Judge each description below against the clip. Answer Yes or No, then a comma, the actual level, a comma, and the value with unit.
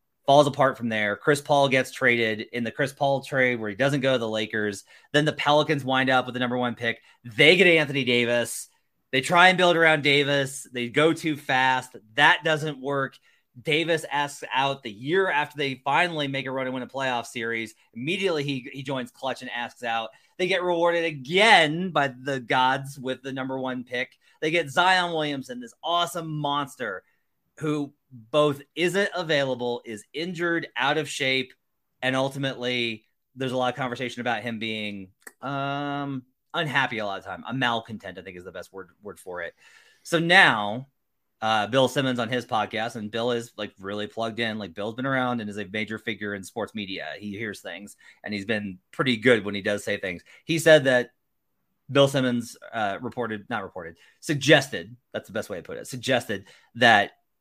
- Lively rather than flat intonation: No, average, 3.9 semitones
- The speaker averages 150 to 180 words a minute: No, average, 195 wpm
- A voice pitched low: Yes, low, 130 Hz